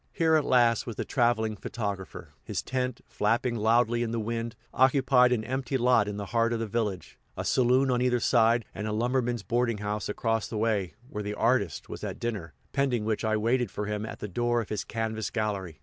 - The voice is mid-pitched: No, low, 115 Hz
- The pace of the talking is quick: Yes, fast, 210 wpm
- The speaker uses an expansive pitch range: No, narrow, 2.6 semitones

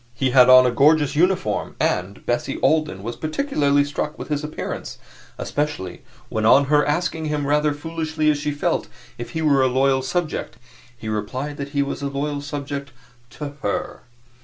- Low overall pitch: No, medium, 145 Hz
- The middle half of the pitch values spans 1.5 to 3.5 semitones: Yes, narrow, 2.4 semitones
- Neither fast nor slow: Yes, average, 175 wpm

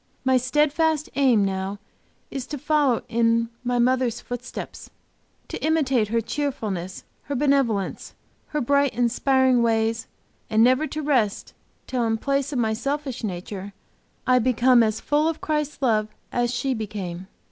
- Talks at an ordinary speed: Yes, average, 145 wpm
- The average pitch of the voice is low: No, high, 245 Hz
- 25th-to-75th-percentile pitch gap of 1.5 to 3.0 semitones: No, average, 4.0 semitones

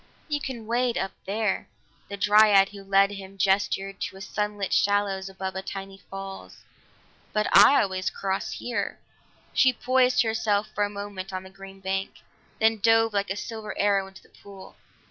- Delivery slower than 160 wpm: No, average, 175 wpm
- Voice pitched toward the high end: Yes, high, 200 Hz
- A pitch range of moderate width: No, narrow, 1.8 semitones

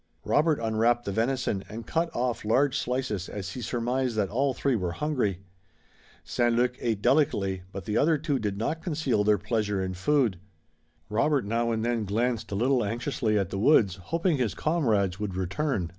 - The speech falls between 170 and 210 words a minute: Yes, average, 180 wpm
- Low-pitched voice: Yes, low, 115 Hz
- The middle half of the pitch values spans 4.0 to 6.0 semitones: Yes, average, 4.8 semitones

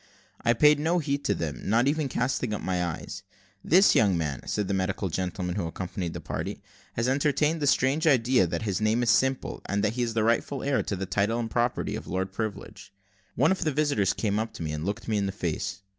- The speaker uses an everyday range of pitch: No, wide, 5.8 semitones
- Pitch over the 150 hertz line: No, low, 110 Hz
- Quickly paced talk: Yes, fast, 235 wpm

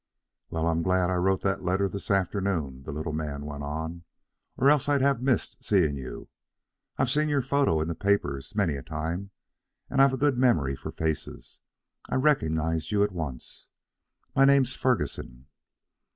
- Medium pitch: No, very low, 90 Hz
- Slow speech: No, average, 170 wpm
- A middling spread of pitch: No, wide, 8.3 semitones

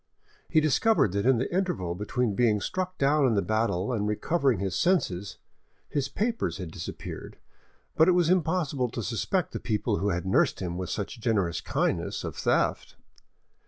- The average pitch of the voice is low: Yes, low, 120 Hz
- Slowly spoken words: No, average, 170 wpm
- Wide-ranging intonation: Yes, wide, 8.1 semitones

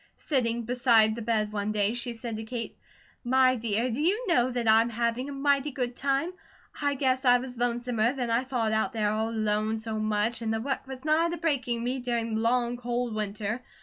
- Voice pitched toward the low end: No, high, 240 Hz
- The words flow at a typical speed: No, fast, 215 wpm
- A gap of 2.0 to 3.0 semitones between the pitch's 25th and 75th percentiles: Yes, average, 2.7 semitones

